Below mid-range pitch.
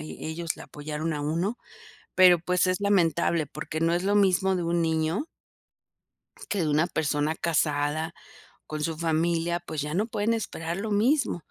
No: medium, 170 Hz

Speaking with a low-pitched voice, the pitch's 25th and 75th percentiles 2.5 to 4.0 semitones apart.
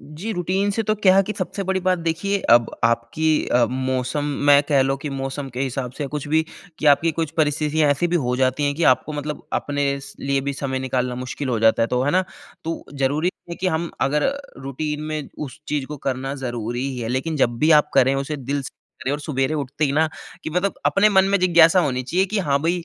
No: medium, 145 Hz; average, 3.7 semitones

